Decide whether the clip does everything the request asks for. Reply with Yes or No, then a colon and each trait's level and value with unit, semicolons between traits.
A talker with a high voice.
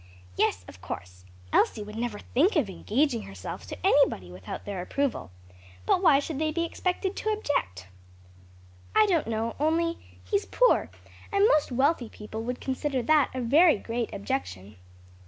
Yes: very high, 255 Hz